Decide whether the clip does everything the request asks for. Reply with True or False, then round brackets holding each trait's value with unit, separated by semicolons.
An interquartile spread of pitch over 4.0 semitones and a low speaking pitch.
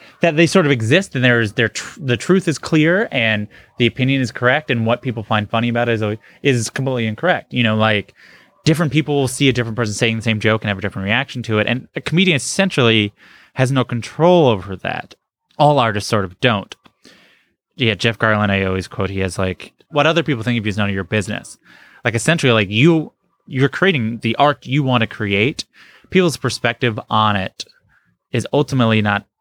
True (4.9 semitones; 120 Hz)